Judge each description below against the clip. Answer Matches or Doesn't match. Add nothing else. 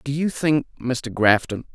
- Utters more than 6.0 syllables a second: Doesn't match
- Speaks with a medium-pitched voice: Doesn't match